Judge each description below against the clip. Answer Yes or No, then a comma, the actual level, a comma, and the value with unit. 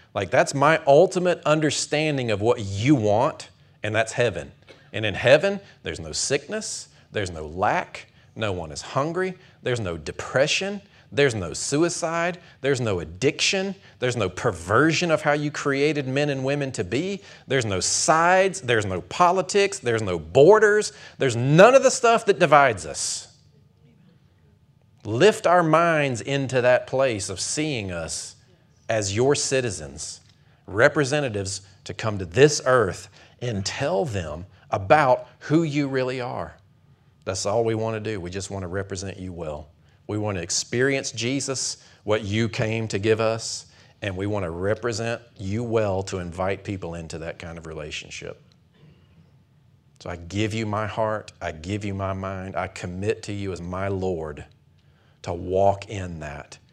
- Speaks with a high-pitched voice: No, low, 115 Hz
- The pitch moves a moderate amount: No, wide, 6.7 semitones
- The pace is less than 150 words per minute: No, average, 160 wpm